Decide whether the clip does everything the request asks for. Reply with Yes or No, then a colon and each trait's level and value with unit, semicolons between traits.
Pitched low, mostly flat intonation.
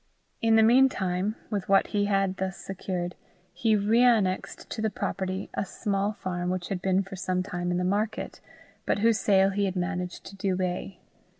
No: high, 195 Hz; narrow, 2.0 semitones